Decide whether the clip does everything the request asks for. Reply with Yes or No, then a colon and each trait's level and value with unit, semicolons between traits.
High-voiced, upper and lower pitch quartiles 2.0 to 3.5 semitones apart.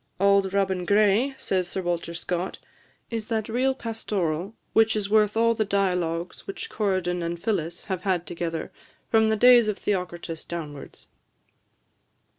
No: high, 195 Hz; average, 3.9 semitones